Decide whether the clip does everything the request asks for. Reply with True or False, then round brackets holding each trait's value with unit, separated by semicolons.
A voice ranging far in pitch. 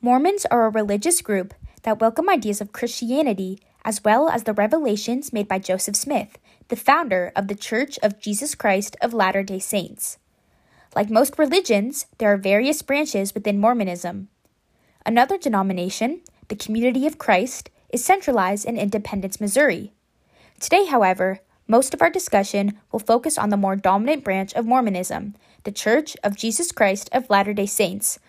False (4.4 semitones)